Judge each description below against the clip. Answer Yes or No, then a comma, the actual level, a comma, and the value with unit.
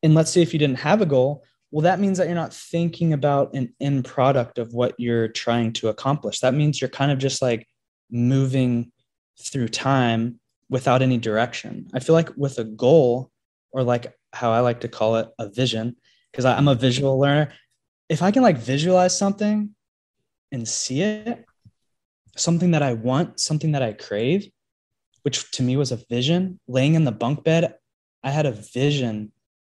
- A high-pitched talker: No, low, 130 Hz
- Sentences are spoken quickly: No, average, 185 wpm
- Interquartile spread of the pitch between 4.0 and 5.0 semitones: Yes, average, 4.5 semitones